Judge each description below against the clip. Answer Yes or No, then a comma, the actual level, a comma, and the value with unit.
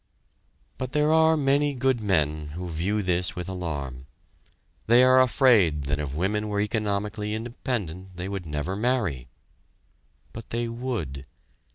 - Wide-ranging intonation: Yes, wide, 6.7 semitones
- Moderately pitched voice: No, low, 100 Hz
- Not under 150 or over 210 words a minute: No, average, 140 wpm